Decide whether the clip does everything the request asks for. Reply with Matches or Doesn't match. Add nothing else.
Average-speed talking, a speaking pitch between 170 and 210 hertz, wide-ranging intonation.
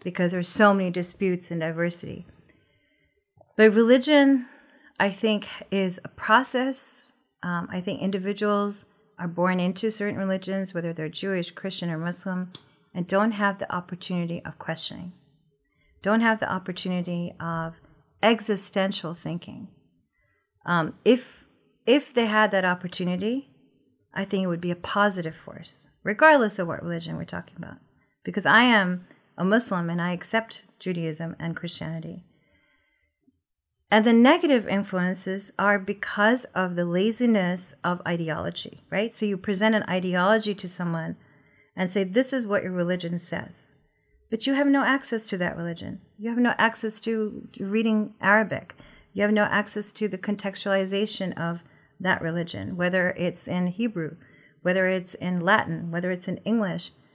Doesn't match